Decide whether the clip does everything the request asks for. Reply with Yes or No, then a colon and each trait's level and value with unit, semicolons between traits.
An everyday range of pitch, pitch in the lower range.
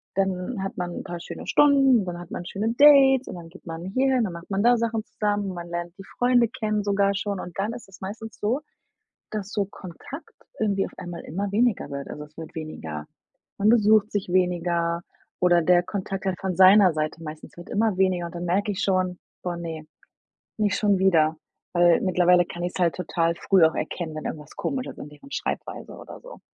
No: average, 3.6 semitones; medium, 185 Hz